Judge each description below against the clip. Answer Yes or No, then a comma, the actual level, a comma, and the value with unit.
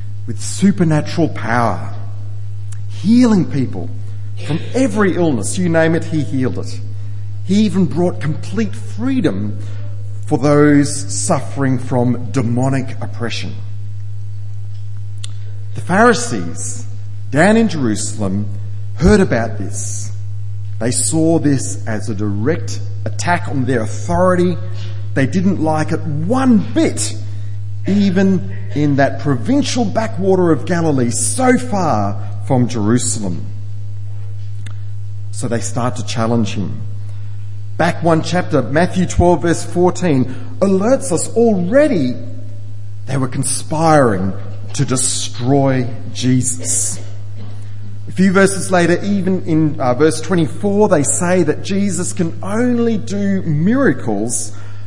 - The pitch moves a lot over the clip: Yes, wide, 7.0 semitones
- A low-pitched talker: Yes, low, 110 Hz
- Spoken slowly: Yes, slow, 110 wpm